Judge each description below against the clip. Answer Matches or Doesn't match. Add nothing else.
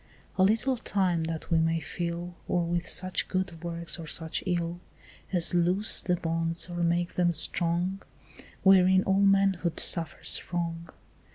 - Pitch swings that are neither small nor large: Doesn't match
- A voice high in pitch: Doesn't match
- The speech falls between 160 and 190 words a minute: Doesn't match